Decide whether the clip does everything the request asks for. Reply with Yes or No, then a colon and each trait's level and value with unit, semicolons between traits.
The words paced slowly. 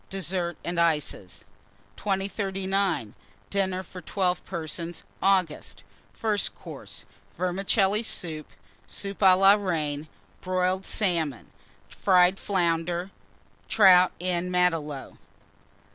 Yes: slow, 90 wpm